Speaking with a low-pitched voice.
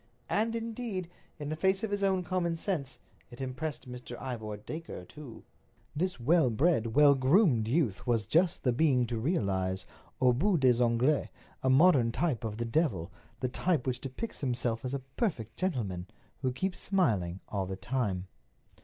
Yes: low, 130 Hz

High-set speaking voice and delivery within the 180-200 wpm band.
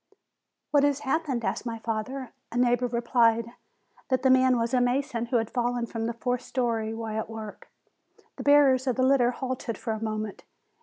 Yes: high, 240 Hz; average, 190 wpm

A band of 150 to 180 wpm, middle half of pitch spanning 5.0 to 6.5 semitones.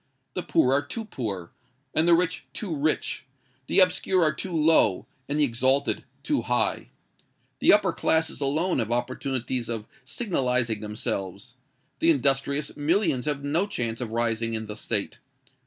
Yes: average, 155 wpm; wide, 5.6 semitones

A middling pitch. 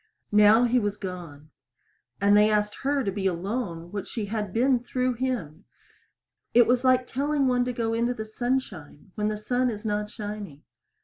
No: high, 215 Hz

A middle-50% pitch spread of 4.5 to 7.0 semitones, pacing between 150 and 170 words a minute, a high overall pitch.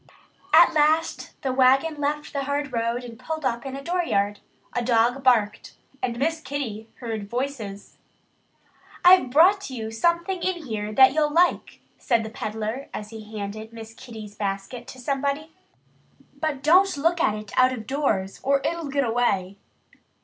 Yes: average, 5.2 semitones; average, 160 wpm; very high, 255 Hz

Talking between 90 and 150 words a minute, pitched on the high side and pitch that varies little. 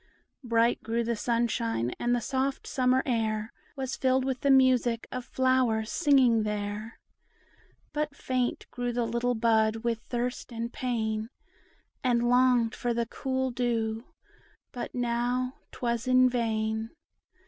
Yes: slow, 135 wpm; high, 240 Hz; narrow, 2.0 semitones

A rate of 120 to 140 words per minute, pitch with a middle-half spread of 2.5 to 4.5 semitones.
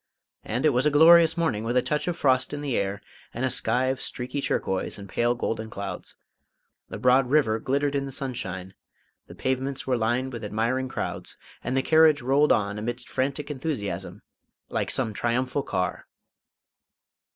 No: average, 175 wpm; average, 3.8 semitones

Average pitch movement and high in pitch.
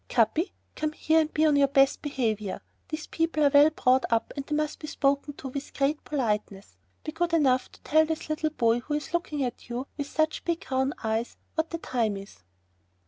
Yes: average, 3.8 semitones; very high, 285 Hz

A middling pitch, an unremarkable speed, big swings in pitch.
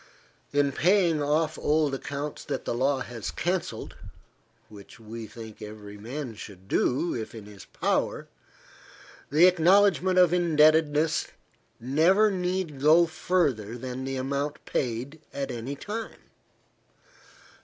No: medium, 145 Hz; slow, 125 wpm; wide, 6.1 semitones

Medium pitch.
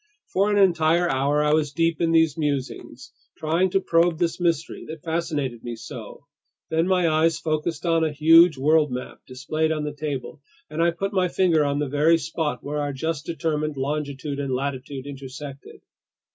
Yes: medium, 155 Hz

